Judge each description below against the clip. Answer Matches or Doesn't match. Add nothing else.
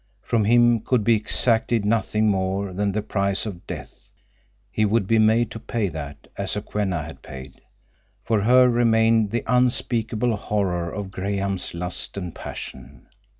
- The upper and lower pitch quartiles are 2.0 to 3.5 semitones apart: Matches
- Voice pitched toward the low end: Matches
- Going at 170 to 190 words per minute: Doesn't match